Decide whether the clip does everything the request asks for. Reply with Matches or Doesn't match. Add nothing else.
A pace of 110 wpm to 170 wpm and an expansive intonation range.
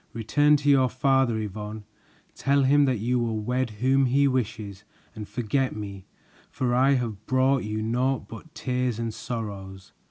Doesn't match